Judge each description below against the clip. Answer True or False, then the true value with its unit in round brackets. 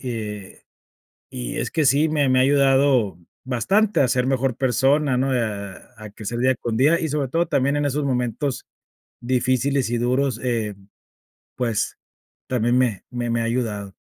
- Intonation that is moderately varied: True (3.1 semitones)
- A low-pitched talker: True (125 Hz)